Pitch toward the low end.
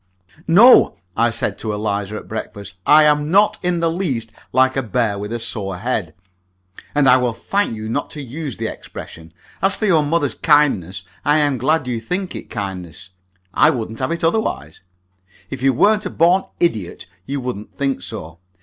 Yes: low, 130 Hz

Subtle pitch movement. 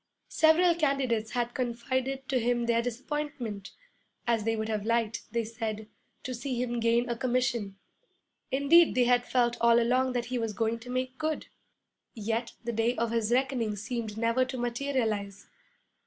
Yes: narrow, 2.2 semitones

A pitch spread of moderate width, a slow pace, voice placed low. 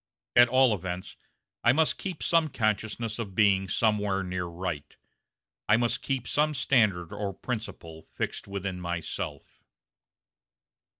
Yes: average, 4.7 semitones; slow, 125 wpm; low, 105 Hz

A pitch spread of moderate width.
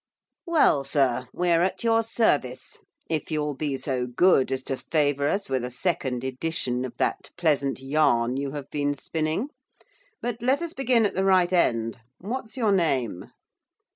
No: wide, 6.3 semitones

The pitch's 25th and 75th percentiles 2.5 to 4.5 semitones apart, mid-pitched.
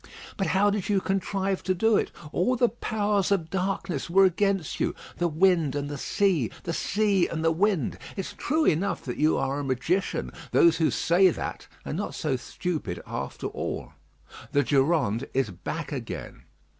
No: average, 5.0 semitones; medium, 175 Hz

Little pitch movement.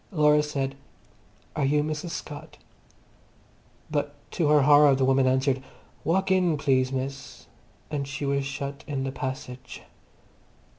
Yes: narrow, 1.9 semitones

